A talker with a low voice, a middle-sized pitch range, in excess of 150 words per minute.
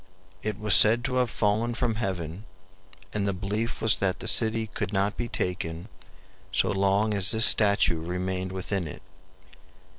Yes: low, 100 Hz; average, 3.1 semitones; average, 160 wpm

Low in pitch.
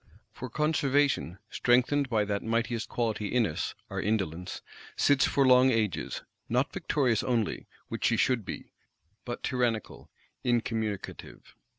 Yes: low, 120 Hz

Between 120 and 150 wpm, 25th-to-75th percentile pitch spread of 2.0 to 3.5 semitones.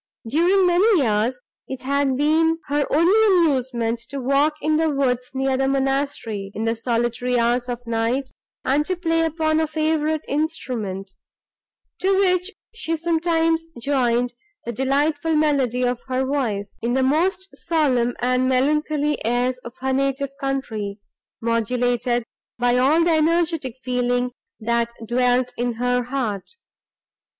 No: average, 140 wpm; average, 4.2 semitones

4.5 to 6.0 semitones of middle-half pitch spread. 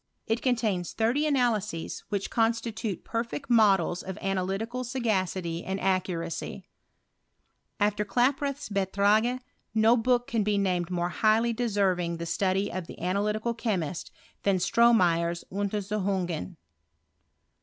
No: average, 3.8 semitones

